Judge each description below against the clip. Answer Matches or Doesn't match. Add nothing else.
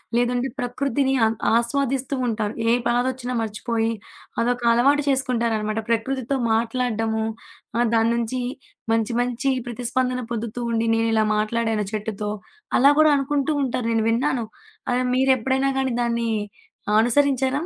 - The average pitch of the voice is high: Matches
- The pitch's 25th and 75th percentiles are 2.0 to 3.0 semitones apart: Matches